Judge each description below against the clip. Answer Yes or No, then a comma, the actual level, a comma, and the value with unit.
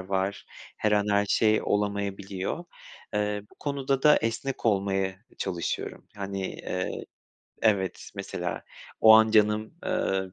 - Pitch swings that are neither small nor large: No, narrow, 2.3 semitones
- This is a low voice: Yes, low, 105 Hz